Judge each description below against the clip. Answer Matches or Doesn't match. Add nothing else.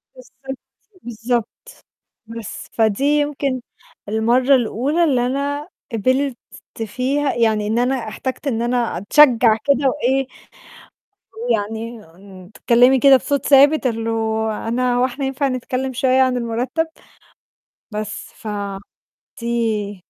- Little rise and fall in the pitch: Doesn't match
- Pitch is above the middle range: Matches